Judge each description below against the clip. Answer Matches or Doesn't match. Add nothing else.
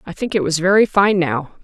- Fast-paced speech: Matches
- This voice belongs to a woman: Matches